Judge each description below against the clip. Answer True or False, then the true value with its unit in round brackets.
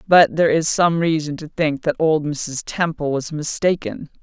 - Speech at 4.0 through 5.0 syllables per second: True (4.6 syllables/s)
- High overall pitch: False (155 Hz)